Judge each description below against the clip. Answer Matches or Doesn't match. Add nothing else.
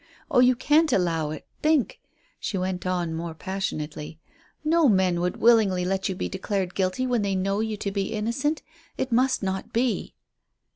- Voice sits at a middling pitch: Doesn't match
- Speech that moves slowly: Doesn't match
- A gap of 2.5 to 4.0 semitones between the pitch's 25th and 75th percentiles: Doesn't match